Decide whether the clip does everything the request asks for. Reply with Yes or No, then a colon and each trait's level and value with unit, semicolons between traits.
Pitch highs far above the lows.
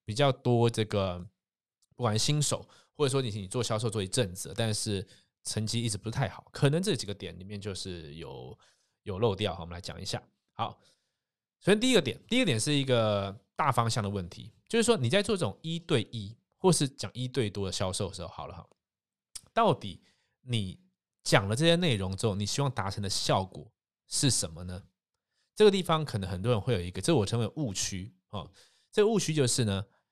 Yes: wide, 5.8 semitones